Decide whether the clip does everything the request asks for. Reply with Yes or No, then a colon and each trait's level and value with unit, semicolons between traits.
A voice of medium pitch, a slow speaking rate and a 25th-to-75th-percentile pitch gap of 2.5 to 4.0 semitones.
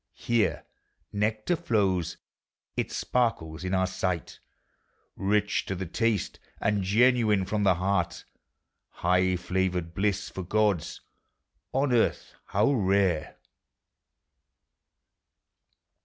No: very low, 95 Hz; slow, 95 wpm; average, 2.8 semitones